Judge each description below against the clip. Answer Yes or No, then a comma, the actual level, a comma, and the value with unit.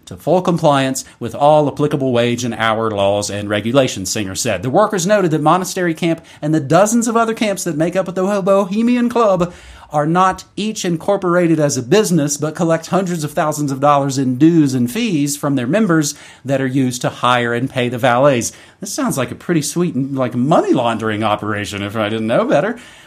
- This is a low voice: No, medium, 150 Hz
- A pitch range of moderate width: No, wide, 6.2 semitones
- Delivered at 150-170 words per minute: No, fast, 205 wpm